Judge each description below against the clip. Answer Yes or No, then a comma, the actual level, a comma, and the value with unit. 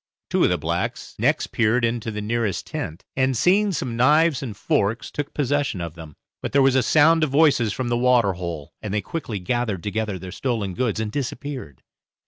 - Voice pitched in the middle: No, low, 120 Hz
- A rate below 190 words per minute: No, average, 195 wpm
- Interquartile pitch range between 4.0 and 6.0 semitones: Yes, average, 5.0 semitones